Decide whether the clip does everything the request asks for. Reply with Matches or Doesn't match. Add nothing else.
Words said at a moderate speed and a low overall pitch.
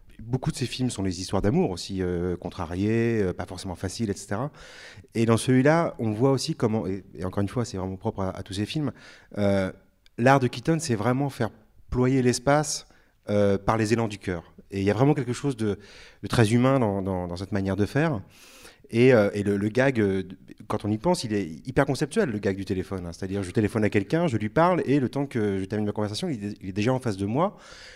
Doesn't match